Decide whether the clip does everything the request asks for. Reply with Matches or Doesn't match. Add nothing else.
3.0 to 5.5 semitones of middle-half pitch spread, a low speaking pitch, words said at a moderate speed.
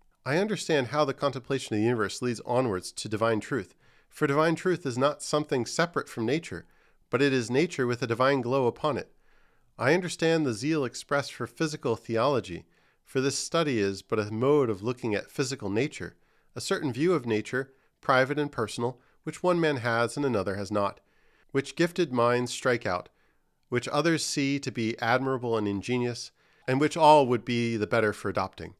Matches